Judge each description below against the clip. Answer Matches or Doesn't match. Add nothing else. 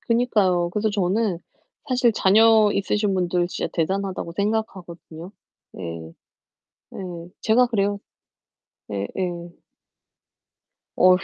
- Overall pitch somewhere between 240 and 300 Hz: Doesn't match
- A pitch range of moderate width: Matches